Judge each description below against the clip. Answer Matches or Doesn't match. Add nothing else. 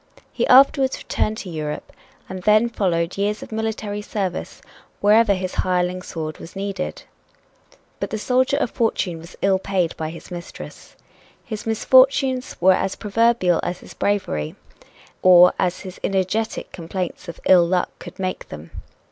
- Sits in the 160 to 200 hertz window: Matches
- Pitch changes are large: Doesn't match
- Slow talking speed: Doesn't match